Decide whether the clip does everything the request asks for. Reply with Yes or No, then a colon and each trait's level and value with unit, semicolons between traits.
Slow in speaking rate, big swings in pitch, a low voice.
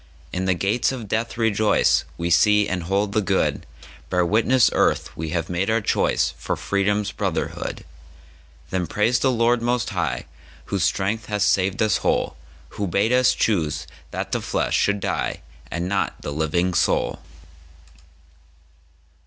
No: slow, 130 wpm; average, 4.2 semitones; low, 100 Hz